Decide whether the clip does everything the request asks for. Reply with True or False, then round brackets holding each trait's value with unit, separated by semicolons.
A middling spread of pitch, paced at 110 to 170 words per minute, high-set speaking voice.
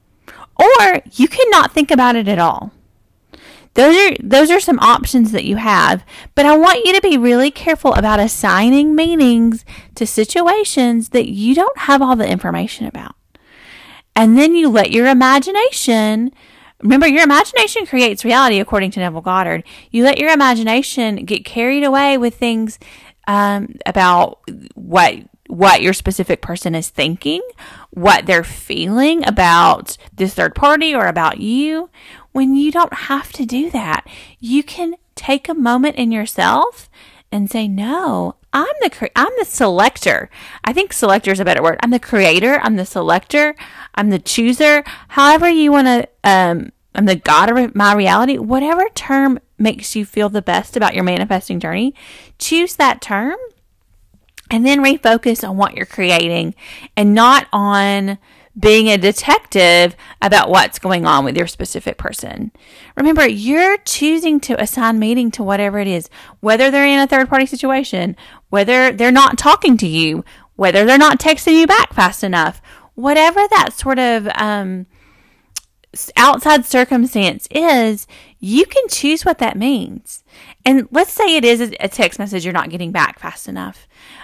False (6.1 semitones; 160 wpm; 245 Hz)